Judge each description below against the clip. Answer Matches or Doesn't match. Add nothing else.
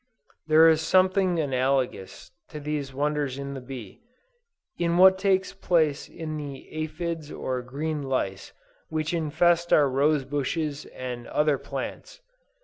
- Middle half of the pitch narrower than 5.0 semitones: Matches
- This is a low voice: Doesn't match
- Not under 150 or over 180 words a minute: Doesn't match